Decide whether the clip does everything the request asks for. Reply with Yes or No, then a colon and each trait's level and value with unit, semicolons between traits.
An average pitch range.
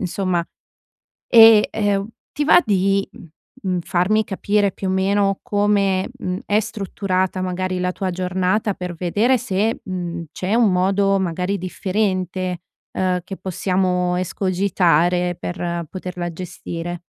No: narrow, 1.8 semitones